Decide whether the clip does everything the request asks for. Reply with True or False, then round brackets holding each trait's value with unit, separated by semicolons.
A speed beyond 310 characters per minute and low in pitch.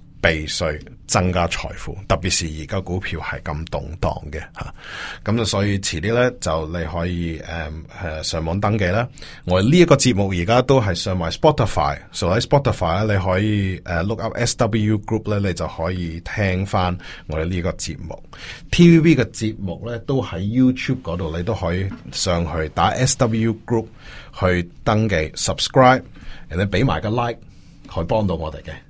True (345 characters per minute; 95 Hz)